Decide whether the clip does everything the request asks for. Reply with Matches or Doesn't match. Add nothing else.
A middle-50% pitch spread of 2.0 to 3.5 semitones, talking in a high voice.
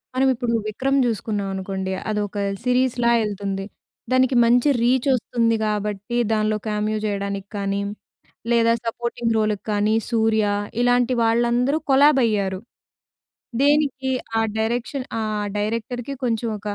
Matches